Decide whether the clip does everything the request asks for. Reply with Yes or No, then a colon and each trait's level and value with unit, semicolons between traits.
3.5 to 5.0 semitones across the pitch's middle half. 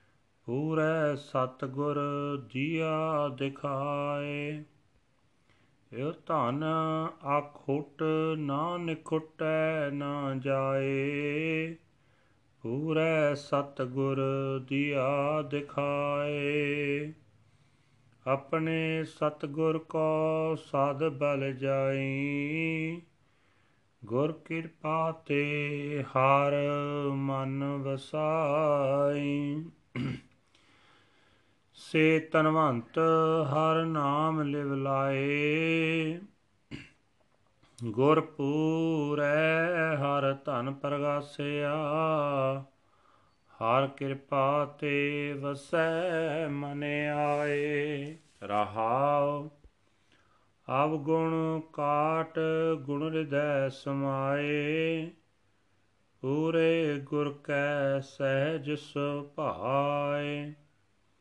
No: narrow, 2.4 semitones